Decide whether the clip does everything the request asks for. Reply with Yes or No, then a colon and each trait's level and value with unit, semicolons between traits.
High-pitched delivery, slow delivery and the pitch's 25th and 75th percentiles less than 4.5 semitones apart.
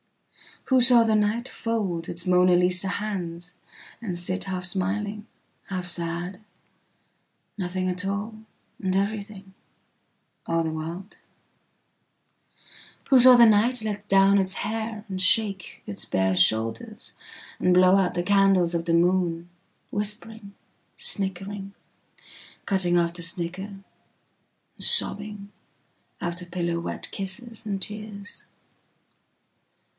Yes: high, 195 Hz; slow, 100 wpm; average, 2.9 semitones